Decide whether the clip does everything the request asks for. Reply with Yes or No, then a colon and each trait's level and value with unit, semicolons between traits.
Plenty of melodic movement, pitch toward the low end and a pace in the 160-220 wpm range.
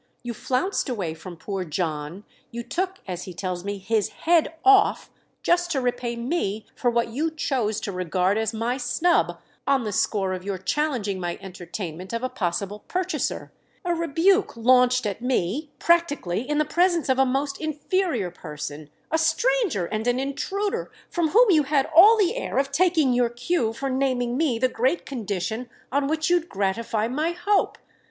No: wide, 8.0 semitones; very high, 250 Hz; average, 175 wpm